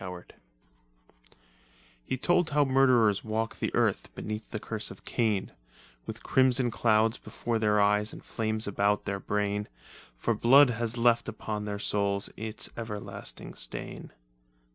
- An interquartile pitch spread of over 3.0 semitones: No, narrow, 2.4 semitones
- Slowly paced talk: No, average, 145 wpm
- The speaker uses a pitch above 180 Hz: No, low, 110 Hz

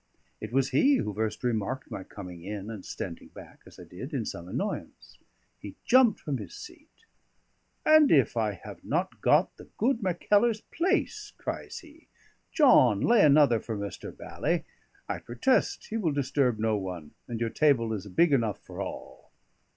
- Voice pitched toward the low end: Yes, low, 125 Hz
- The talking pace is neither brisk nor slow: Yes, average, 170 wpm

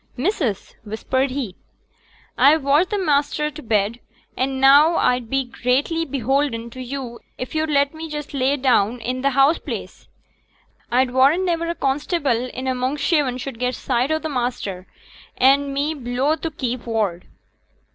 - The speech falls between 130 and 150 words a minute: No, average, 165 wpm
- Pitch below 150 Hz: No, very high, 270 Hz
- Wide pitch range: No, average, 3.1 semitones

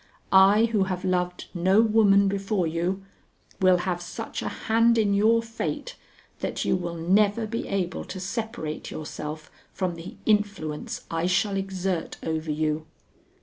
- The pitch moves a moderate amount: Yes, average, 3.3 semitones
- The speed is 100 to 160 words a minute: Yes, average, 145 wpm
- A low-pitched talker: No, high, 190 Hz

